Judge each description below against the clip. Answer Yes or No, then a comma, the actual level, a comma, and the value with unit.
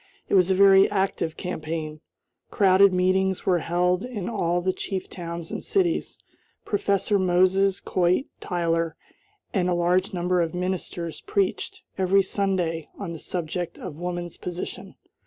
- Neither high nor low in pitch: Yes, medium, 180 Hz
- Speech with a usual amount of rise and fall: No, narrow, 1.9 semitones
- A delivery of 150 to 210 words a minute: No, average, 140 wpm